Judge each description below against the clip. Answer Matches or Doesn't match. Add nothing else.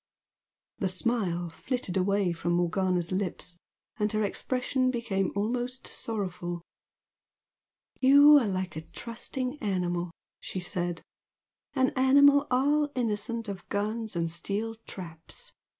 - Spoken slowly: Matches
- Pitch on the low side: Doesn't match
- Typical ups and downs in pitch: Doesn't match